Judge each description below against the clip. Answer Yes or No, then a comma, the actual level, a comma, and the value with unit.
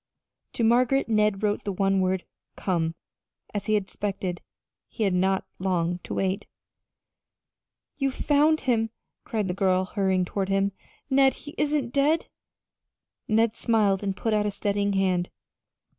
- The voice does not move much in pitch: No, average, 3.3 semitones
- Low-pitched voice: No, high, 200 Hz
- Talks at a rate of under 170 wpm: Yes, average, 150 wpm